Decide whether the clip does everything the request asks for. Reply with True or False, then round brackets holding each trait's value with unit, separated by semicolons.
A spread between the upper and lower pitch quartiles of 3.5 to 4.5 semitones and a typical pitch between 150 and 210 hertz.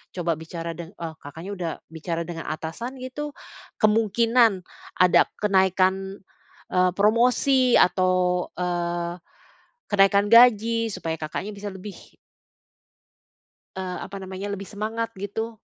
True (4.0 semitones; 190 Hz)